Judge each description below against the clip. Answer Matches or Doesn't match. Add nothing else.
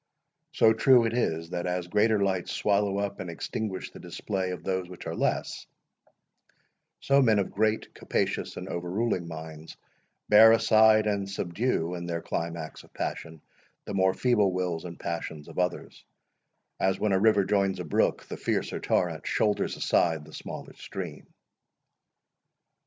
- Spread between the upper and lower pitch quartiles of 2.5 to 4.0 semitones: Matches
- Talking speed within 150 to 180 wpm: Matches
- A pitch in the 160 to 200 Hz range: Doesn't match